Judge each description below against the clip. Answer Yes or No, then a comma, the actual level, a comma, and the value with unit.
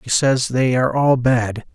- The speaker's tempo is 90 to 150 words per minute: No, fast, 205 wpm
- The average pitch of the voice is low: Yes, low, 125 Hz